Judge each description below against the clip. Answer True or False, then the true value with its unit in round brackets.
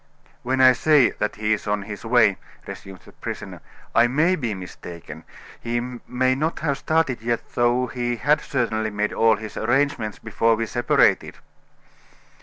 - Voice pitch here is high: False (120 Hz)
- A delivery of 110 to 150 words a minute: False (160 wpm)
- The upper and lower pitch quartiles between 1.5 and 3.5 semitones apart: True (3.2 semitones)